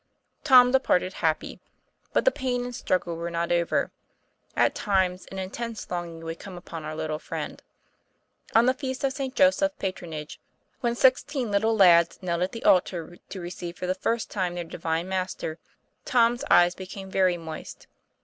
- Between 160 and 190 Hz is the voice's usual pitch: Yes, medium, 185 Hz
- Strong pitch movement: Yes, wide, 5.7 semitones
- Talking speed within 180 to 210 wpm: No, average, 170 wpm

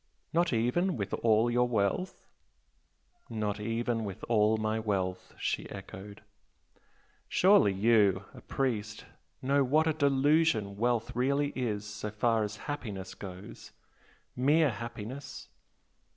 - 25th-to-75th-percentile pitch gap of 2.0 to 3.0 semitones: No, average, 4.5 semitones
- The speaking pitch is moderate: No, low, 115 Hz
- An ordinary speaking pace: No, slow, 120 wpm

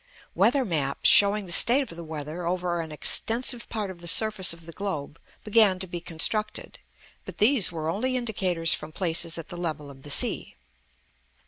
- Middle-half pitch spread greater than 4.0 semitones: Yes, average, 4.6 semitones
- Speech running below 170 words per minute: No, average, 185 wpm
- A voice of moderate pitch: Yes, medium, 175 Hz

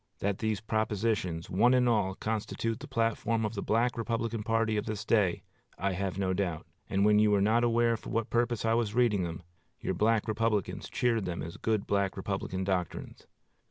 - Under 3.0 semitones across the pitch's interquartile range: Yes, narrow, 2.6 semitones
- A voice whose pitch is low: Yes, low, 110 Hz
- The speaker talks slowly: No, average, 195 wpm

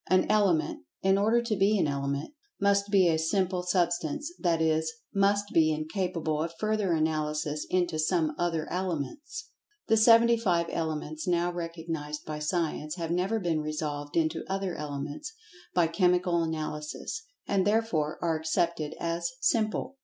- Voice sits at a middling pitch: Yes, medium, 170 Hz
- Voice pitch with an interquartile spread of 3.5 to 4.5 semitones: Yes, average, 3.9 semitones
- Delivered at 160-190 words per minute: No, average, 145 wpm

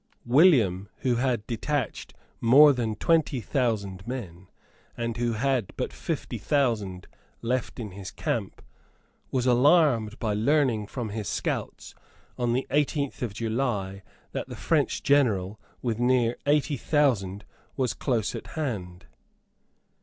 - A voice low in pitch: Yes, low, 120 Hz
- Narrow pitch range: No, average, 4.3 semitones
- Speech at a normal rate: No, slow, 130 wpm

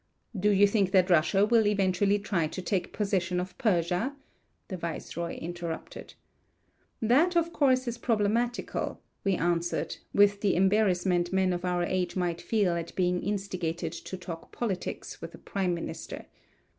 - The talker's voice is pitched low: No, high, 190 Hz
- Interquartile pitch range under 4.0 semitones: Yes, average, 3.0 semitones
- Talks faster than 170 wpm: No, average, 150 wpm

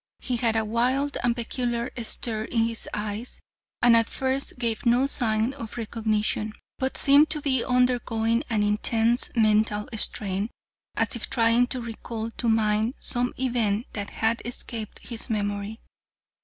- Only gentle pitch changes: Yes, narrow, 2.1 semitones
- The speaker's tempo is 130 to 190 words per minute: Yes, average, 150 wpm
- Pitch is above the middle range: Yes, high, 230 Hz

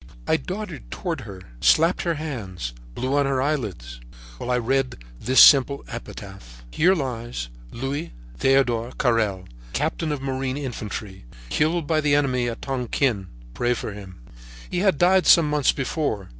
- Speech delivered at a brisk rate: No, average, 150 wpm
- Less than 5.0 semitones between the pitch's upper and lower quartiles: No, wide, 5.4 semitones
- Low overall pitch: Yes, low, 130 Hz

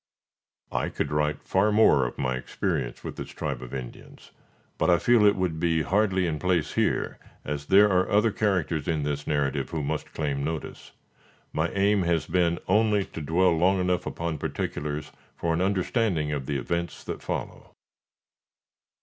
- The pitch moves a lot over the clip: No, average, 4.2 semitones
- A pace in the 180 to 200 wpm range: No, average, 170 wpm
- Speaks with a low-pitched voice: Yes, very low, 85 Hz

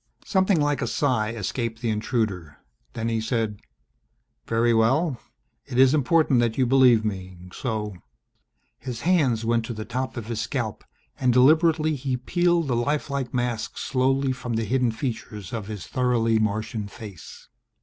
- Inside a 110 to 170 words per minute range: Yes, average, 160 wpm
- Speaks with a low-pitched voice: Yes, low, 120 Hz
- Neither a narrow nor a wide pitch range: Yes, average, 3.3 semitones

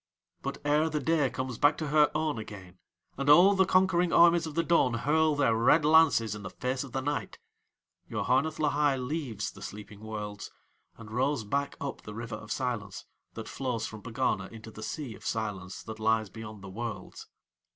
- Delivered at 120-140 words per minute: No, average, 190 wpm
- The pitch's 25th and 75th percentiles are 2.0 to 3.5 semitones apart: No, wide, 5.5 semitones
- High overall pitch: No, low, 130 Hz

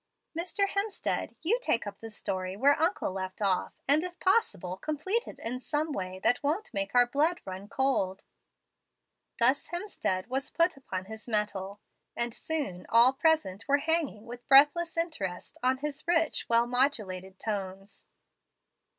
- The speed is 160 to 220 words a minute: No, average, 150 wpm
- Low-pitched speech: No, very high, 250 Hz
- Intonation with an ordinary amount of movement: No, wide, 8.3 semitones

